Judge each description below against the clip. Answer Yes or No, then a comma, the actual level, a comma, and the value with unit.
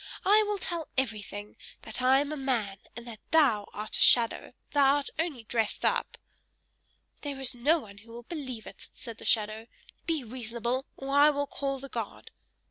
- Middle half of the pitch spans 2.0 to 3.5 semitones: No, average, 4.2 semitones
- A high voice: Yes, very high, 255 Hz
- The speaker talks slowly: No, average, 185 wpm